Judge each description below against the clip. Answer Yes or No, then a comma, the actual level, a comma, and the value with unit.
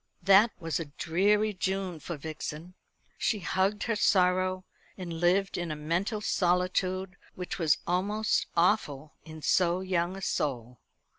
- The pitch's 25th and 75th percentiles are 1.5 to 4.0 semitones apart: Yes, average, 2.9 semitones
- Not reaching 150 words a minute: Yes, average, 140 wpm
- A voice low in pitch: No, medium, 180 Hz